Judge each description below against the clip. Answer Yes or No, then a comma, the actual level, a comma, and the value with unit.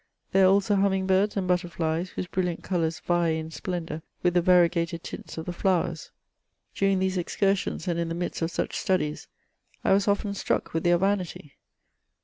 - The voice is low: No, medium, 180 Hz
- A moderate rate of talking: Yes, average, 180 wpm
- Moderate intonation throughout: No, narrow, 2.3 semitones